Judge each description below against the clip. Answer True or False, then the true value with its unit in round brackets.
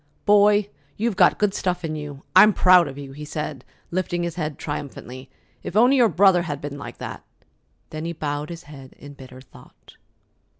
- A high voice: False (155 Hz)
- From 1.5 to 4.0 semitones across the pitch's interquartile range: False (4.5 semitones)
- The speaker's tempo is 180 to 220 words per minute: True (185 wpm)